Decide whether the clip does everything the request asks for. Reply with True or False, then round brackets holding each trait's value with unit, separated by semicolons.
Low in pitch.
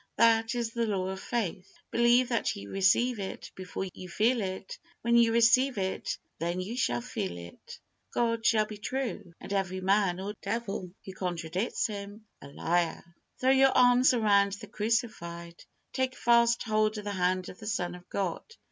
False (205 Hz)